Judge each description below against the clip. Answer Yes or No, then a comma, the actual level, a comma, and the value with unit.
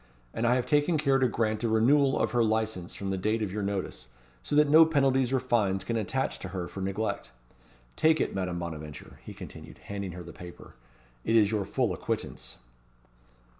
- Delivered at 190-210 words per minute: Yes, average, 200 wpm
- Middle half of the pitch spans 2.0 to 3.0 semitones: No, wide, 5.4 semitones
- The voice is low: Yes, low, 110 Hz